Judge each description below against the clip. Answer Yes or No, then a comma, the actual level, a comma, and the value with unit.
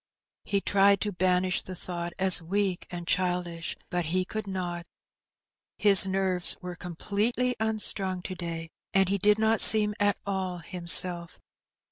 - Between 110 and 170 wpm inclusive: Yes, average, 145 wpm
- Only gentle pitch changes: Yes, narrow, 2.2 semitones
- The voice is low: No, medium, 185 Hz